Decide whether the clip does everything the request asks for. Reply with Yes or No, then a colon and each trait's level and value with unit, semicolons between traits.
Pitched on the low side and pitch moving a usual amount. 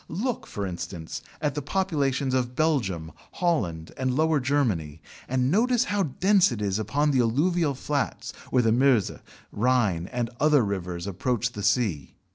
No: low, 125 Hz; wide, 6.6 semitones